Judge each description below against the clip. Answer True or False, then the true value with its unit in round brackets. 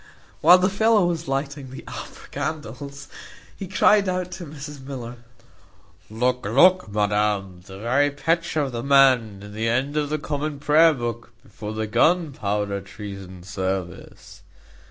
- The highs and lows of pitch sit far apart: True (6.5 semitones)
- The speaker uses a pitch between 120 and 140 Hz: True (135 Hz)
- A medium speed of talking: True (145 wpm)